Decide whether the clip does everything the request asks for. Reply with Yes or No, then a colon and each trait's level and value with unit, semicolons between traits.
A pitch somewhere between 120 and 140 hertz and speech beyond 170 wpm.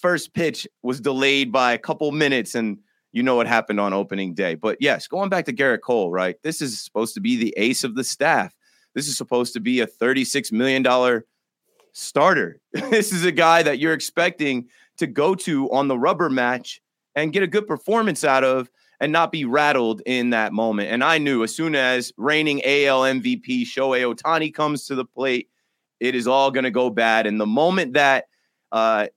Yes: low, 135 Hz; average, 200 wpm